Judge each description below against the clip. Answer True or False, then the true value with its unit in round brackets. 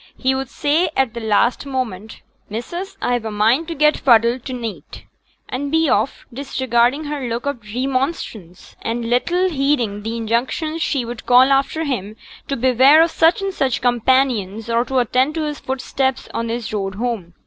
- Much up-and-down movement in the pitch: False (3.5 semitones)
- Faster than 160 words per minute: True (175 wpm)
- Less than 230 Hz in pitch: False (255 Hz)